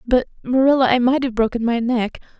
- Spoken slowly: No, average, 200 wpm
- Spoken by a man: No, female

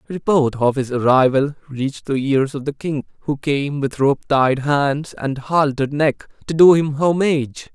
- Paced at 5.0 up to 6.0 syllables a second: No, 4.5 syllables/s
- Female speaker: No, male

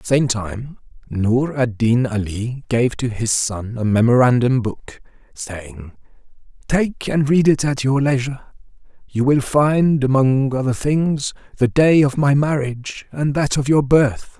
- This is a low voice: Yes, low, 130 Hz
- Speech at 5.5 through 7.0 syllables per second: No, 4.0 syllables/s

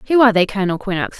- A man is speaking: No, female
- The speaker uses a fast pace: Yes, fast, 250 wpm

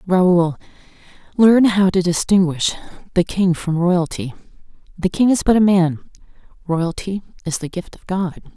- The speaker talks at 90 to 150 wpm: Yes, average, 145 wpm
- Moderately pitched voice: Yes, medium, 180 Hz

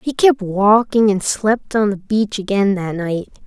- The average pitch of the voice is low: No, high, 205 Hz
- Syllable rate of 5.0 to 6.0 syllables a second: No, 4.0 syllables/s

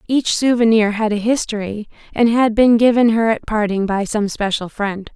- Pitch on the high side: Yes, high, 220 Hz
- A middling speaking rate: Yes, average, 185 wpm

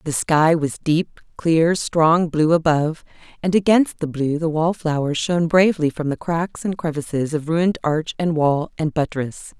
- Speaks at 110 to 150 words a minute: No, average, 175 wpm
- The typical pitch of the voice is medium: Yes, medium, 160 Hz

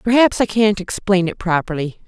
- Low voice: No, high, 195 Hz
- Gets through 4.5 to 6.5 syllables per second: Yes, 5.2 syllables/s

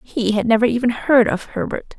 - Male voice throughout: No, female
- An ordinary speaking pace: No, fast, 210 wpm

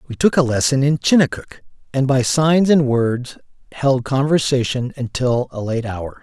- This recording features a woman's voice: No, male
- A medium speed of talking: Yes, average, 165 wpm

